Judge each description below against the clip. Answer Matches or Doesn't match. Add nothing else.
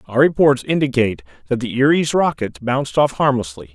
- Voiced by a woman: Doesn't match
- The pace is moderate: Matches